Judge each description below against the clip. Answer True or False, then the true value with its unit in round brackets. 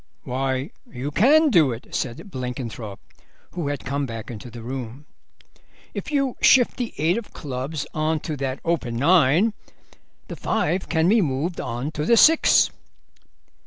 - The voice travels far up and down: True (5.8 semitones)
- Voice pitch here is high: False (145 Hz)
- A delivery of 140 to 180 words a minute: True (155 wpm)